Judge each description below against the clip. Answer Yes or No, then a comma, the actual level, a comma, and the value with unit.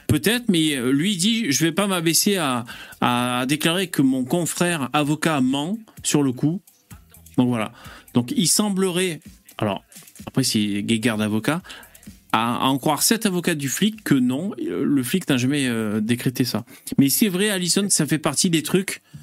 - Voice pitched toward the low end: No, medium, 150 Hz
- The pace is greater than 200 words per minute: No, average, 170 wpm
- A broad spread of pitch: Yes, wide, 6.6 semitones